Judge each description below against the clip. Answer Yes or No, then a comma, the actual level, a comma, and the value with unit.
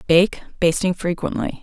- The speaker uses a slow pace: Yes, slow, 110 wpm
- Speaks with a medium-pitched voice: Yes, medium, 180 Hz